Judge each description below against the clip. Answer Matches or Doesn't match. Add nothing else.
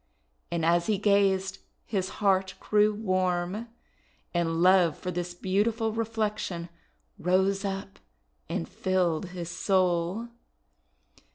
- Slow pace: Matches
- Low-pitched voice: Doesn't match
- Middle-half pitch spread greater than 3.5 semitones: Doesn't match